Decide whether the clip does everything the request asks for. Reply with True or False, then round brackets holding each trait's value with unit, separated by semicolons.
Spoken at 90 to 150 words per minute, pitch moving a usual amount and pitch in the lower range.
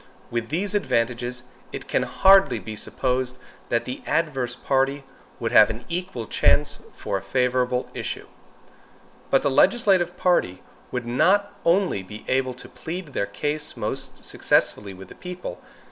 False (145 wpm; 6.6 semitones; 130 Hz)